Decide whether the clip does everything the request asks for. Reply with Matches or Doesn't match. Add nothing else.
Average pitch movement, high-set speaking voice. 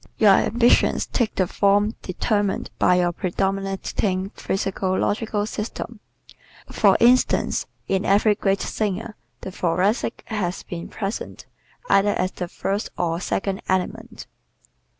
Doesn't match